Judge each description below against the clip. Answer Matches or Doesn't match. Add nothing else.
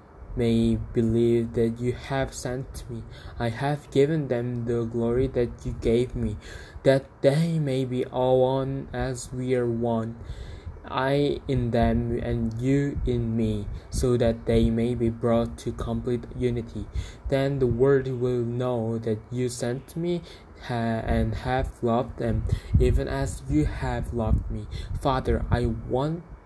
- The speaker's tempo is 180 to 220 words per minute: Doesn't match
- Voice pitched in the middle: Doesn't match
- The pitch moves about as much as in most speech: Doesn't match